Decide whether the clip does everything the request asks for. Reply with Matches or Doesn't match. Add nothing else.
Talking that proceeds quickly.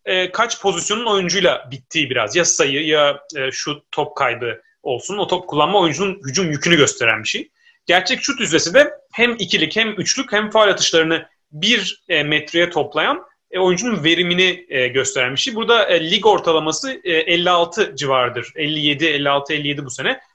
Matches